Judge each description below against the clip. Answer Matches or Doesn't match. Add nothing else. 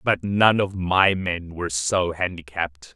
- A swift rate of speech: Doesn't match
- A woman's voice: Doesn't match